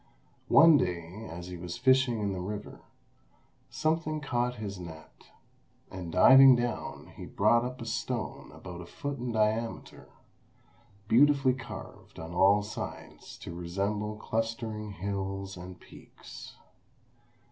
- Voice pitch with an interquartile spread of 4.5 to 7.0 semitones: Yes, average, 5.0 semitones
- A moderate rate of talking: No, slow, 125 wpm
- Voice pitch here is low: Yes, low, 105 Hz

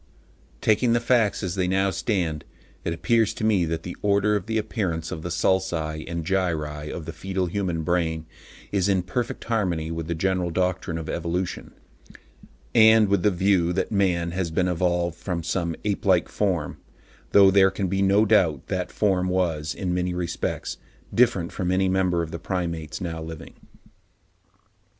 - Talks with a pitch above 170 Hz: No, very low, 90 Hz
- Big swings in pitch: No, average, 2.7 semitones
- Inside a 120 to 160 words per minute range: No, average, 175 wpm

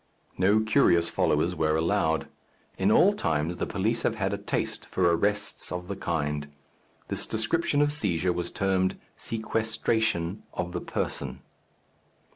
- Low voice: Yes, very low, 95 Hz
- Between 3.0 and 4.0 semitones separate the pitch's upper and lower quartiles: No, average, 4.6 semitones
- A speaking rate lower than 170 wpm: Yes, average, 140 wpm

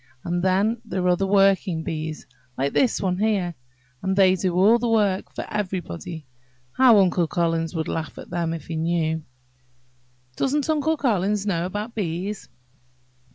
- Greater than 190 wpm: No, average, 155 wpm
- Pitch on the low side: No, medium, 185 Hz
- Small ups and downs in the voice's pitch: No, average, 3.7 semitones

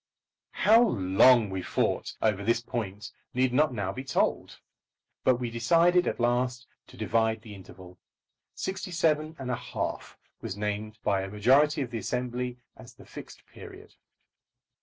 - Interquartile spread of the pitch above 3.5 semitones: Yes, average, 4.2 semitones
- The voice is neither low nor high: No, low, 120 Hz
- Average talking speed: Yes, average, 155 wpm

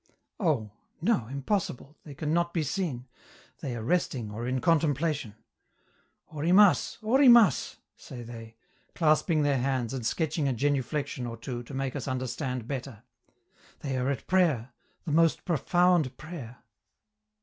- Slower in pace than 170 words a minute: Yes, average, 140 wpm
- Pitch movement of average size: Yes, average, 4.8 semitones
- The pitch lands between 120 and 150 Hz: Yes, medium, 140 Hz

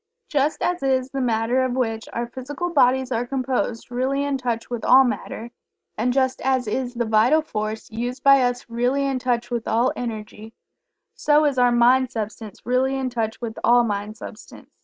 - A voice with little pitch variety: Yes, narrow, 2.3 semitones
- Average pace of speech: Yes, average, 185 wpm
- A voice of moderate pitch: No, high, 245 Hz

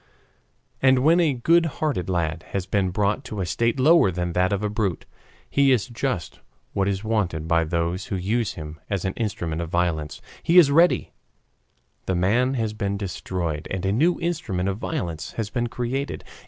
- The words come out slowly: No, average, 185 wpm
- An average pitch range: No, wide, 6.3 semitones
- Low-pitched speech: Yes, low, 100 Hz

